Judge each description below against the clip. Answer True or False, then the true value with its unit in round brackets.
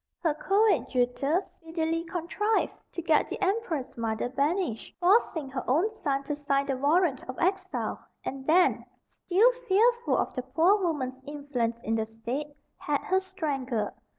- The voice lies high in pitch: True (300 Hz)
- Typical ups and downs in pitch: False (6.0 semitones)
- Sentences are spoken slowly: False (150 wpm)